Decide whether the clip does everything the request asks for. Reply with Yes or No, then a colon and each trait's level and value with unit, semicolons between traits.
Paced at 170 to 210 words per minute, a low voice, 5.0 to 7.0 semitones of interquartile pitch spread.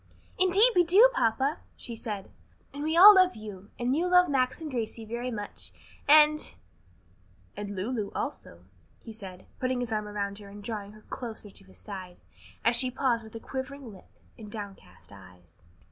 No: average, 180 wpm; high, 225 Hz; average, 5.3 semitones